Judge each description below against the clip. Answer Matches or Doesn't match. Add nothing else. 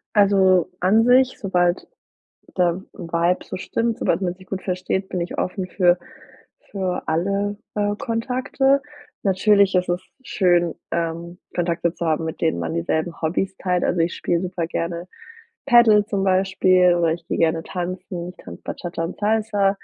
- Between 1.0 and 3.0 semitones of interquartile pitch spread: Matches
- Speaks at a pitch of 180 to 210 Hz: Matches